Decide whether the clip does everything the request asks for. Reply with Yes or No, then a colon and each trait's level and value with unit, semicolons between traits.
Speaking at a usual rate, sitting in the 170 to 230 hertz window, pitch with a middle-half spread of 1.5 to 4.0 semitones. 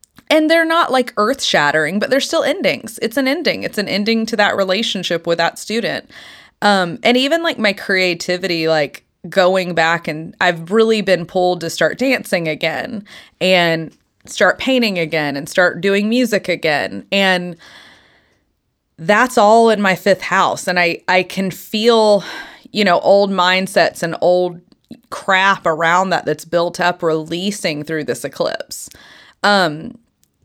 No: average, 155 wpm; high, 190 Hz; average, 4.8 semitones